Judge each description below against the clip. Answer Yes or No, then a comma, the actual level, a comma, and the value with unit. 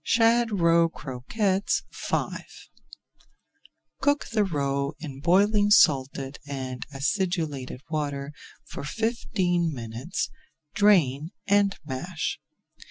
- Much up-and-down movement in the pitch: Yes, wide, 6.5 semitones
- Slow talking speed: Yes, slow, 90 wpm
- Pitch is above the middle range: No, medium, 165 Hz